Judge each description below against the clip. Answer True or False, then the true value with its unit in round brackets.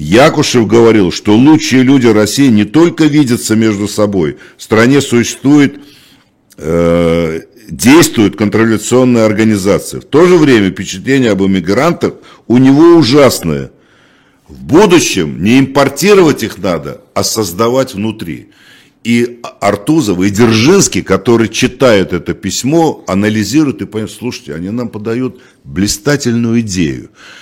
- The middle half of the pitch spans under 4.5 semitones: False (4.8 semitones)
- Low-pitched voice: True (115 Hz)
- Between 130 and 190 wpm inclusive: False (120 wpm)